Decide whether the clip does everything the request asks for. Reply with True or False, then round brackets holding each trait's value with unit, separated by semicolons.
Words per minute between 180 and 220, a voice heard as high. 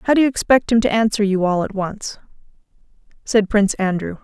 True (200 wpm; 210 Hz)